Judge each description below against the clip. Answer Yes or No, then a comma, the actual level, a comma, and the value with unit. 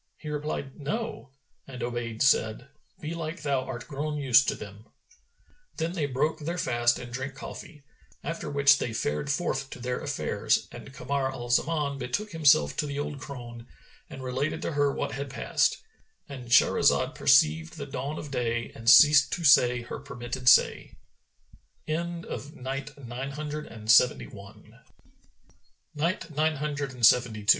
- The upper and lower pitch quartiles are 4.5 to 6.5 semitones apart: No, average, 3.2 semitones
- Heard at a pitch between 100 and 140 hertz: Yes, low, 135 Hz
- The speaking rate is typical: No, slow, 130 wpm